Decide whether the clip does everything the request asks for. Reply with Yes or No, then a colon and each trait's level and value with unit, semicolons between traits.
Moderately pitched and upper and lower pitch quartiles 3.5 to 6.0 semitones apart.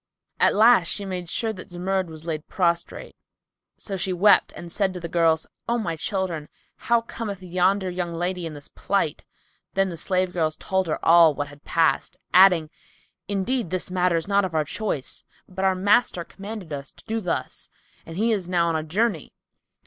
No: medium, 180 Hz; average, 2.9 semitones